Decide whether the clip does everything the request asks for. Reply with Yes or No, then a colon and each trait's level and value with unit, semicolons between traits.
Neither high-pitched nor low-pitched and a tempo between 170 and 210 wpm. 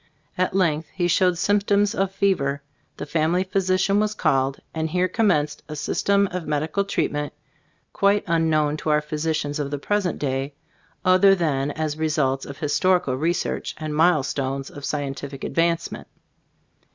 No: medium, 160 Hz; average, 160 wpm